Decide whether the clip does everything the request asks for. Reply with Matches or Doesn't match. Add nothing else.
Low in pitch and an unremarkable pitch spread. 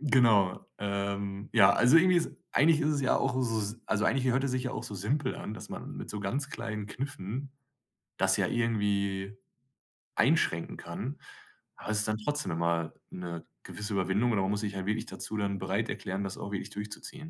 Matches